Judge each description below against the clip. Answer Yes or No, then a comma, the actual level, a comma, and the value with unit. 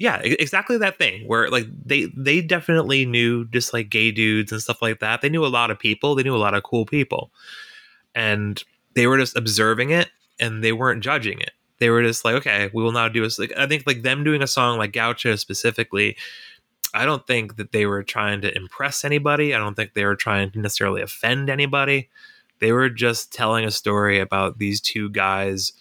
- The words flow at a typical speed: No, fast, 215 wpm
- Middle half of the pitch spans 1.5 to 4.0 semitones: No, average, 4.5 semitones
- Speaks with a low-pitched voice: Yes, low, 115 Hz